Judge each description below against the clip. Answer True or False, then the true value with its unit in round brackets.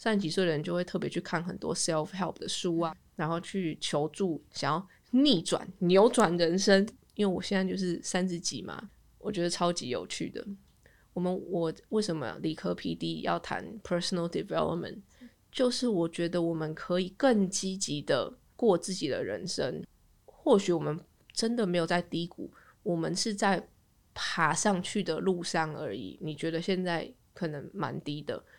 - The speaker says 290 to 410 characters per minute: True (295 characters per minute)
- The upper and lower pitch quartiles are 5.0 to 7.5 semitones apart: False (3.0 semitones)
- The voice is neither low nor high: True (175 Hz)